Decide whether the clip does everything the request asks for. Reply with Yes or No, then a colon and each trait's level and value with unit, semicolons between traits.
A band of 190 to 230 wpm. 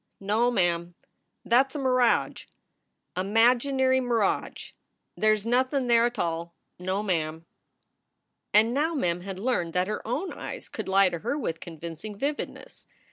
No: average, 160 wpm